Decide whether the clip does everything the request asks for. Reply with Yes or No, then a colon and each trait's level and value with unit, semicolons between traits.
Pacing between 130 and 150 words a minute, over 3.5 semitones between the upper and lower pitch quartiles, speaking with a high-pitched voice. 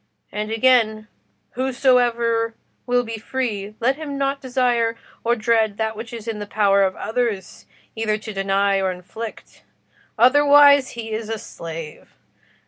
No: average, 145 wpm; average, 2.7 semitones; high, 225 Hz